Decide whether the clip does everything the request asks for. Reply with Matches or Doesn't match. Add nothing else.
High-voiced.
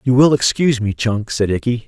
Doesn't match